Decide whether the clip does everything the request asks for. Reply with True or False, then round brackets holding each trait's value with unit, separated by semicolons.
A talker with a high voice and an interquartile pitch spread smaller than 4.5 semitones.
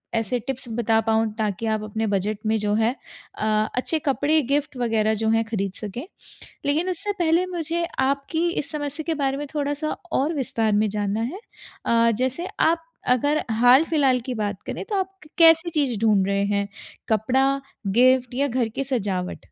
False (250 Hz; 5.2 semitones)